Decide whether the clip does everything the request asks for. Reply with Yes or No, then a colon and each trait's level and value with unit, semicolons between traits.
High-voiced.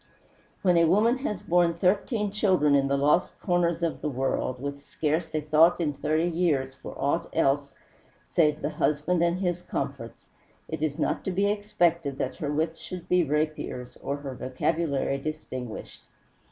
No: medium, 160 Hz